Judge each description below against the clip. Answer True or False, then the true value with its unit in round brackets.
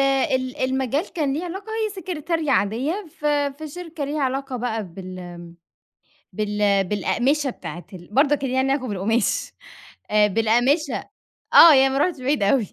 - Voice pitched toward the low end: False (265 Hz)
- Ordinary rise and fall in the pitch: False (5.9 semitones)